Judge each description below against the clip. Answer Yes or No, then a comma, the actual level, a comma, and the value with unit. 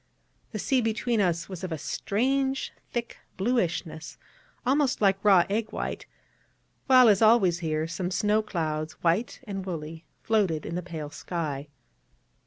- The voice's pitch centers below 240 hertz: Yes, high, 190 Hz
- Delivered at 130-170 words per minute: Yes, average, 140 wpm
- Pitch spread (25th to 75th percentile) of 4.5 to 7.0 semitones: Yes, wide, 5.4 semitones